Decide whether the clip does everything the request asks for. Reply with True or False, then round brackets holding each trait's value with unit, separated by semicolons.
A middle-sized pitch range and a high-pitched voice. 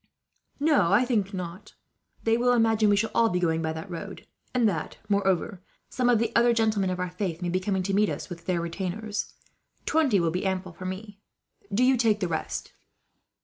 True (3.8 semitones; 200 Hz)